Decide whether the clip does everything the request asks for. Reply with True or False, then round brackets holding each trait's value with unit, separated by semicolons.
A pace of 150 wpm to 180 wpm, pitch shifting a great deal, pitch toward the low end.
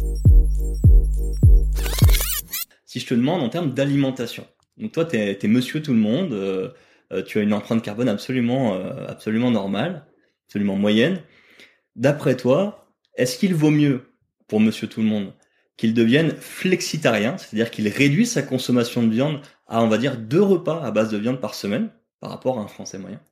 True (170 wpm; 6.1 semitones; 125 Hz)